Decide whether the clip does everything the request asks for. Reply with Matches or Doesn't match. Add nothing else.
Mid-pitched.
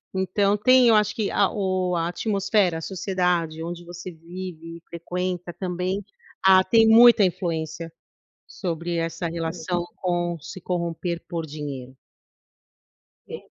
Matches